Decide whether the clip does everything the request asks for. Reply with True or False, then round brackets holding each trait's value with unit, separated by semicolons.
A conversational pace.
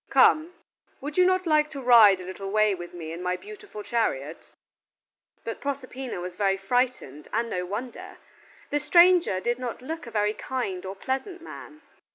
True (175 wpm)